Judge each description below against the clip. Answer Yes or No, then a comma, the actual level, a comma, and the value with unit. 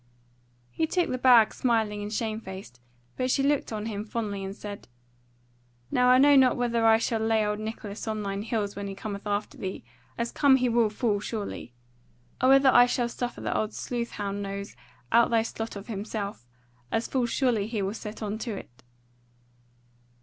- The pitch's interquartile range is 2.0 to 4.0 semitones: Yes, average, 2.9 semitones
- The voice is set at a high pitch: Yes, high, 220 Hz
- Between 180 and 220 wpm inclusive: Yes, average, 190 wpm